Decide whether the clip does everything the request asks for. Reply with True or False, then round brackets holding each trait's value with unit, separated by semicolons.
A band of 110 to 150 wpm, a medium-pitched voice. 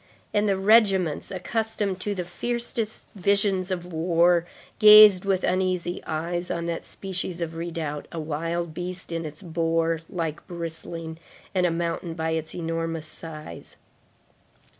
True (140 wpm; 175 Hz)